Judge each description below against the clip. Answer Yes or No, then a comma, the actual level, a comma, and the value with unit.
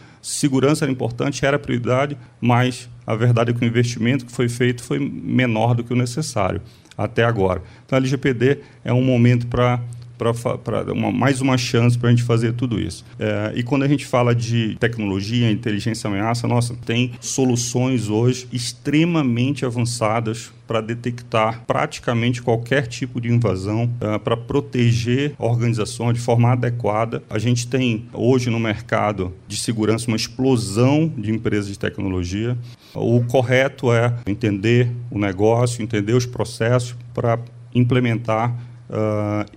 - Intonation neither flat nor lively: No, narrow, 2.0 semitones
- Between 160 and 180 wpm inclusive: No, average, 145 wpm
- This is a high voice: No, low, 120 Hz